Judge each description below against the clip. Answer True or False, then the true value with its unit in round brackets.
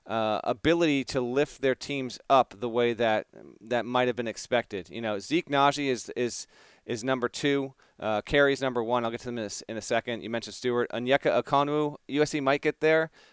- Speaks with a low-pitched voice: True (125 Hz)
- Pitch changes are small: False (3.3 semitones)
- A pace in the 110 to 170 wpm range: False (205 wpm)